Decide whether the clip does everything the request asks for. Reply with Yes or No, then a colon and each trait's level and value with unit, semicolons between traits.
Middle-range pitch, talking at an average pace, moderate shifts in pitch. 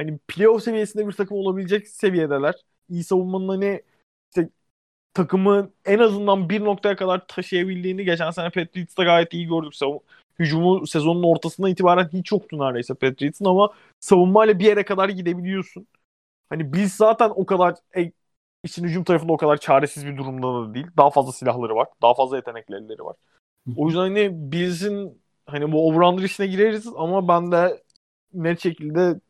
No: medium, 180 Hz; fast, 155 wpm; average, 3.8 semitones